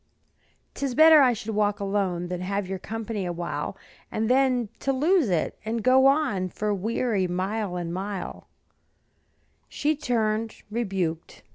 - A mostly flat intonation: No, average, 4.9 semitones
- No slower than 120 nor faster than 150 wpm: Yes, average, 140 wpm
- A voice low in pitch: No, high, 215 Hz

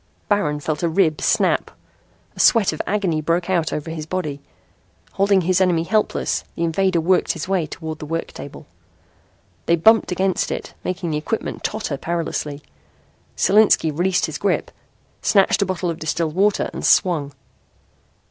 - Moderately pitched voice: Yes, medium, 170 Hz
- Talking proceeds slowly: No, average, 155 wpm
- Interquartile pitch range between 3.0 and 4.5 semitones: Yes, average, 3.3 semitones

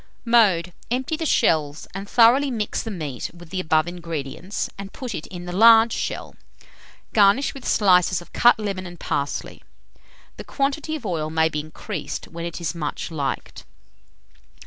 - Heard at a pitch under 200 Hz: Yes, medium, 185 Hz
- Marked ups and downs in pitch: Yes, wide, 5.8 semitones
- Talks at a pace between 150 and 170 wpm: Yes, average, 165 wpm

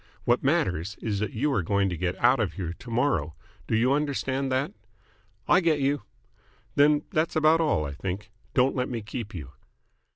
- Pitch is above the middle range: No, low, 120 Hz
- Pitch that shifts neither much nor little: No, wide, 6.5 semitones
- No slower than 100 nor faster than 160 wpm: No, average, 190 wpm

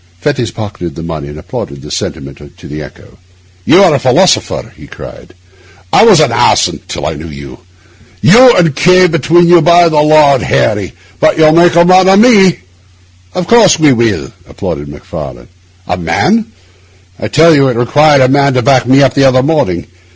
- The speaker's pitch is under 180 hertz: Yes, medium, 140 Hz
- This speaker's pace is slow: No, average, 190 wpm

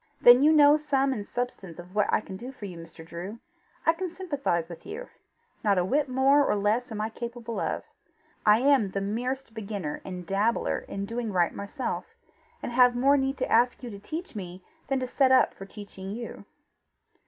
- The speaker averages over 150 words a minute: Yes, average, 200 wpm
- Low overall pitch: No, high, 230 Hz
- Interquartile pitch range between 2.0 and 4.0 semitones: No, average, 5.3 semitones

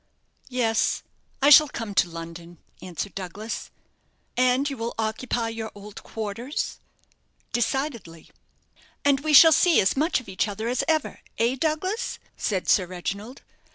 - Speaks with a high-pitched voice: Yes, high, 230 Hz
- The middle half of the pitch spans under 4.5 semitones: No, wide, 5.5 semitones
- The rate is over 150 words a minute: No, average, 140 wpm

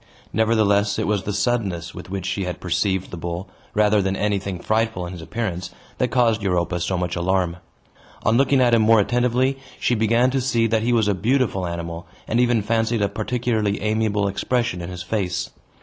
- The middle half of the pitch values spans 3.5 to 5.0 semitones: Yes, average, 3.9 semitones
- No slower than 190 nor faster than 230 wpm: Yes, average, 195 wpm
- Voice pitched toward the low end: Yes, low, 105 Hz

